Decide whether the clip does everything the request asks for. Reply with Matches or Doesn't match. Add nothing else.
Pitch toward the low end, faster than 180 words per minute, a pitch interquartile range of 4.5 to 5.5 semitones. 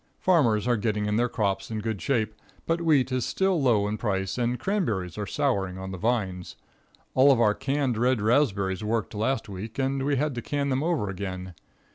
Matches